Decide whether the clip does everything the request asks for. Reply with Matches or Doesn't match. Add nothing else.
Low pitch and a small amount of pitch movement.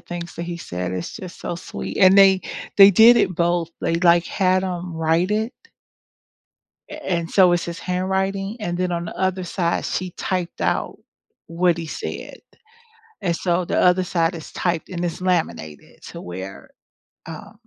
Doesn't match